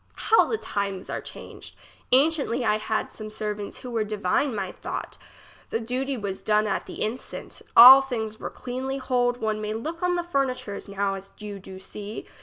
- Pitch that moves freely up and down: No, average, 3.9 semitones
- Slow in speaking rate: No, average, 190 wpm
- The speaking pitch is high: Yes, high, 220 Hz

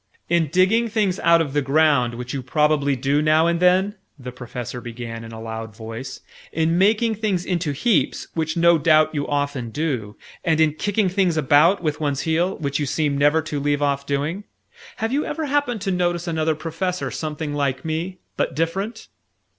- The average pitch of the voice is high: No, medium, 155 Hz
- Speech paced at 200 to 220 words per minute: No, average, 185 wpm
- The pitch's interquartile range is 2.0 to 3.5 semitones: No, average, 4.3 semitones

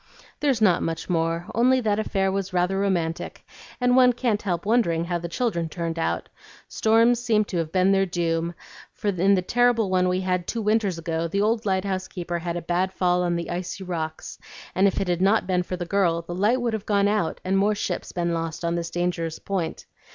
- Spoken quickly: Yes, fast, 215 wpm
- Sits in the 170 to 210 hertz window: Yes, medium, 185 Hz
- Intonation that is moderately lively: Yes, average, 3.4 semitones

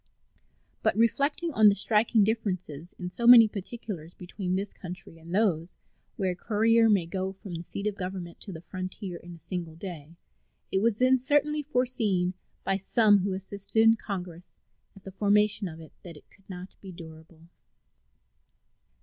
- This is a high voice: Yes, high, 195 Hz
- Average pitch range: Yes, average, 3.7 semitones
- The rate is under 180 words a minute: Yes, average, 170 wpm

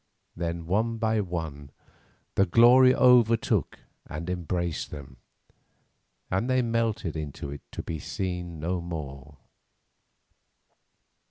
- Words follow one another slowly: Yes, slow, 105 wpm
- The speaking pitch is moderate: No, very low, 90 Hz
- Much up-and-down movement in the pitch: Yes, wide, 6.3 semitones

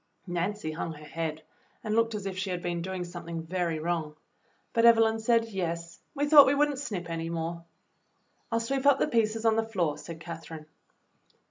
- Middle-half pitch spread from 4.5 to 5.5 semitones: Yes, average, 5.2 semitones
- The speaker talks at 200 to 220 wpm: Yes, fast, 205 wpm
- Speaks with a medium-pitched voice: Yes, medium, 180 Hz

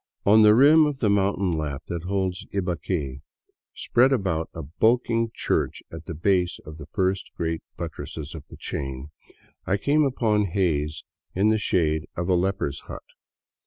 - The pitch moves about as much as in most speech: Yes, average, 4.9 semitones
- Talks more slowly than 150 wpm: No, average, 160 wpm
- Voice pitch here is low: Yes, very low, 95 Hz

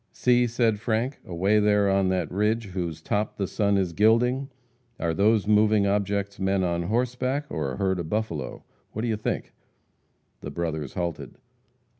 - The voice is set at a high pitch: No, low, 100 Hz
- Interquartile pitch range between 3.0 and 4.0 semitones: Yes, average, 3.4 semitones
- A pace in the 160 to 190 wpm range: Yes, average, 165 wpm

